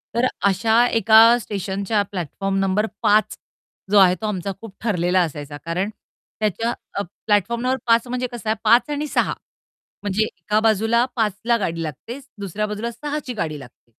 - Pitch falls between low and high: No, high, 210 Hz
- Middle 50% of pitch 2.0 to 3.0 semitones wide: No, average, 3.4 semitones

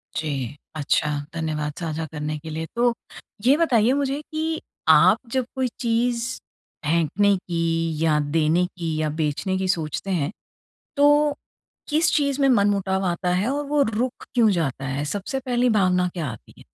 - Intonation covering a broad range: Yes, wide, 7.9 semitones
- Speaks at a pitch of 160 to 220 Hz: Yes, high, 190 Hz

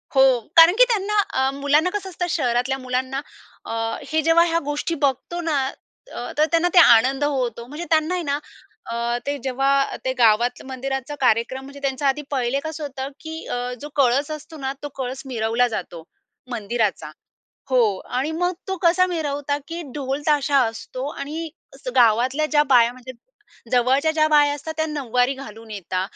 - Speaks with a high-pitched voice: Yes, very high, 275 Hz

